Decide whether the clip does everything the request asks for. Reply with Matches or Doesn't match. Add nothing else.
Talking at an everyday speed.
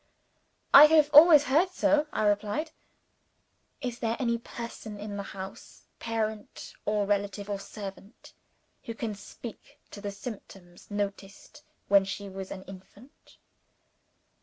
Doesn't match